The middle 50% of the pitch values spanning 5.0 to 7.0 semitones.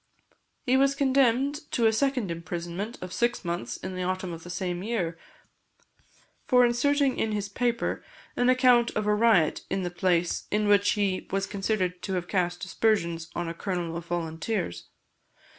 Yes: average, 5.3 semitones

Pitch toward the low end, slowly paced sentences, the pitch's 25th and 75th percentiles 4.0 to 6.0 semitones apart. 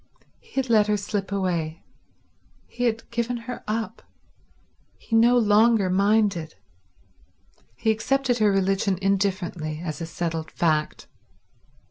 No: high, 205 Hz; slow, 120 wpm; average, 4.3 semitones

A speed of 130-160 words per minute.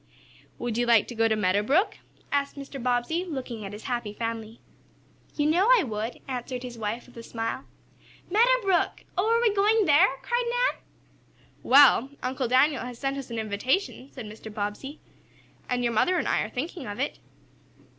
No: average, 185 wpm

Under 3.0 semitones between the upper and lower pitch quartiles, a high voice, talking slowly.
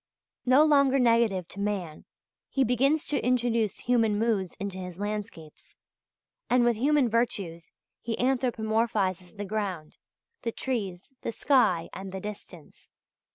No: average, 4.5 semitones; high, 220 Hz; slow, 130 wpm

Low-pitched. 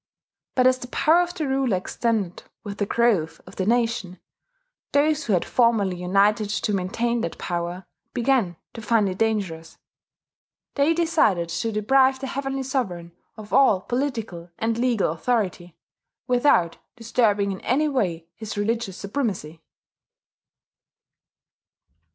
No: high, 220 Hz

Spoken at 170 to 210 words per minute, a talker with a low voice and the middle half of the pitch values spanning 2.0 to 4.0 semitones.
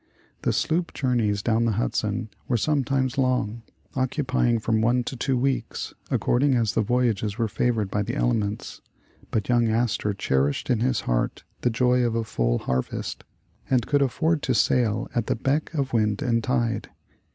Yes: average, 175 wpm; low, 120 Hz; average, 2.9 semitones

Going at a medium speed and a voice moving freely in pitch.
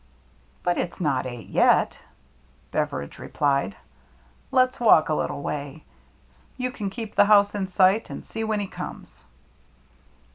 Yes: average, 150 wpm; wide, 7.2 semitones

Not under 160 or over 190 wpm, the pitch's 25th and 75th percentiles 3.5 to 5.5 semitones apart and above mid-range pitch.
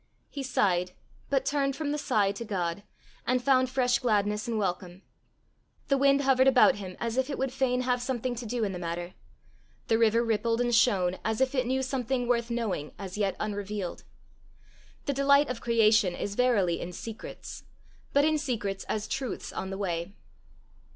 Yes: average, 180 wpm; average, 4.5 semitones; high, 230 Hz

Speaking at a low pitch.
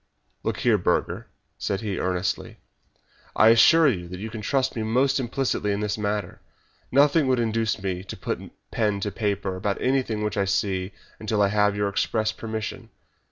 Yes: low, 105 Hz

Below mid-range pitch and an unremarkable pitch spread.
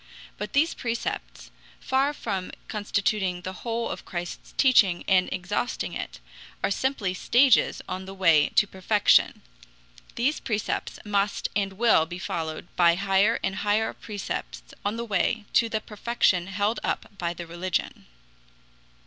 No: high, 200 Hz; average, 3.8 semitones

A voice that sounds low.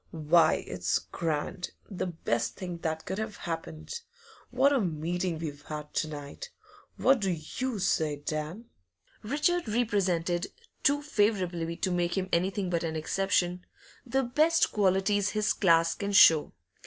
No: medium, 180 Hz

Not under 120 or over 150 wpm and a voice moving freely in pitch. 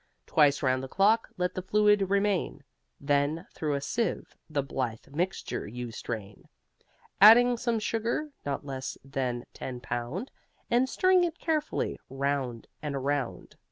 Yes: average, 140 wpm; wide, 8.2 semitones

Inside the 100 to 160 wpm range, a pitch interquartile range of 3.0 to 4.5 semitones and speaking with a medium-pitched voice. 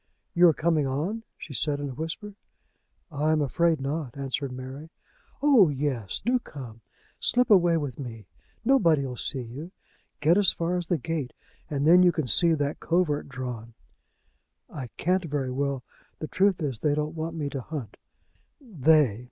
No: average, 170 wpm; average, 4.1 semitones; medium, 150 Hz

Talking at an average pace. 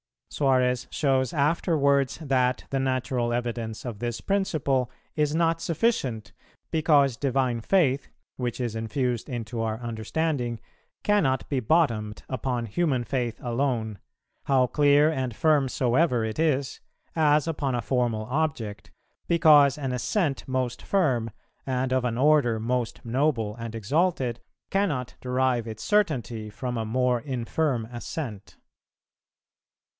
No: slow, 125 wpm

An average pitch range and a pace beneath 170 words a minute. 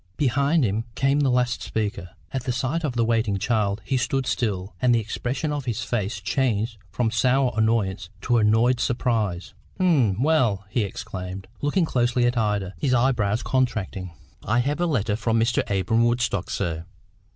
No: average, 3.7 semitones; average, 175 wpm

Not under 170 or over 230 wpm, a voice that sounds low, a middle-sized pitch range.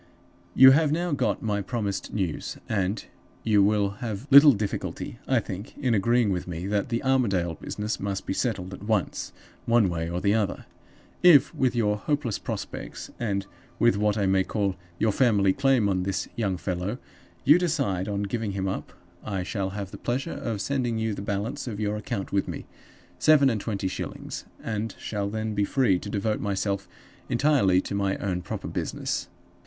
Yes: average, 180 wpm; low, 105 Hz; average, 3.4 semitones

